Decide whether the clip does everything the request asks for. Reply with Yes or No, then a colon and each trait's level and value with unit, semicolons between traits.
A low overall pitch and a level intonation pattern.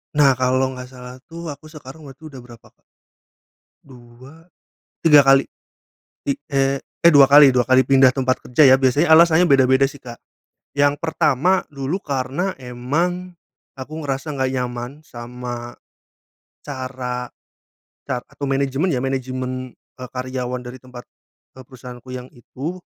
Yes: low, 130 Hz; narrow, 2.2 semitones